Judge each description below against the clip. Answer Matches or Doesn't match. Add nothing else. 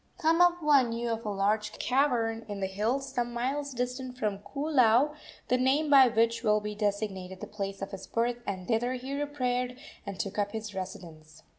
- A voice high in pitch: Matches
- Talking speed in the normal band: Matches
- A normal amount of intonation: Matches